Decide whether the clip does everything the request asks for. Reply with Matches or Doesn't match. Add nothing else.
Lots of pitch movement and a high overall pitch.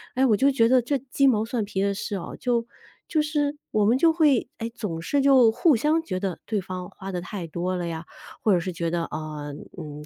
Matches